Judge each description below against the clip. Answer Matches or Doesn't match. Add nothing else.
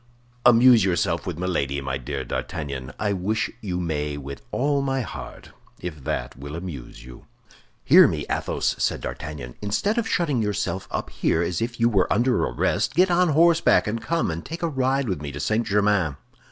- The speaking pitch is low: Matches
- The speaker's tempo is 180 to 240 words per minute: Matches